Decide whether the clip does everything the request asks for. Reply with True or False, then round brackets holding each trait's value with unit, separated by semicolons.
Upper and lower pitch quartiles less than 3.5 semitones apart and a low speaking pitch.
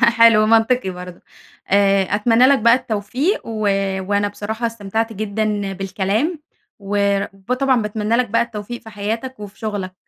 False (2.4 semitones; 215 Hz)